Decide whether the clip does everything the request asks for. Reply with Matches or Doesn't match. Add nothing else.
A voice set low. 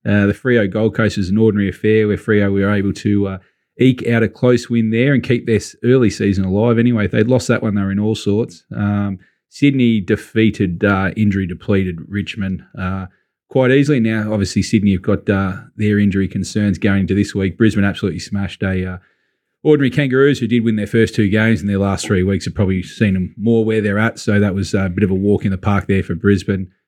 Matches